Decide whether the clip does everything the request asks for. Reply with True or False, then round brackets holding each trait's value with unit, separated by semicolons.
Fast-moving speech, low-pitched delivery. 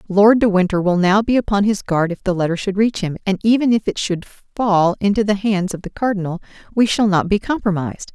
False (235 wpm; 200 Hz)